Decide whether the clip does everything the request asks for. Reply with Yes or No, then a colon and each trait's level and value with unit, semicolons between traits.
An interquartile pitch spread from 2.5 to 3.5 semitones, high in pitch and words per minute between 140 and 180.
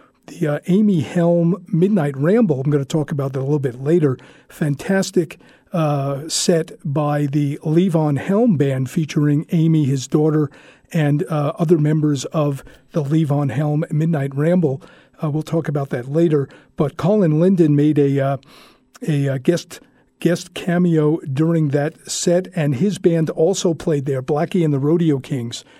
No: average, 3.0 semitones; medium, 155 Hz; average, 160 wpm